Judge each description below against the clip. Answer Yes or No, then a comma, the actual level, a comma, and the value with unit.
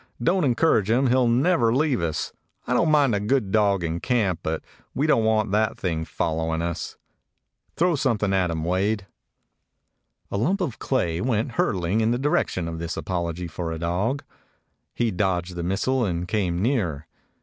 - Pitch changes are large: Yes, wide, 6.3 semitones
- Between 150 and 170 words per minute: No, average, 180 wpm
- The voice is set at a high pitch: No, low, 105 Hz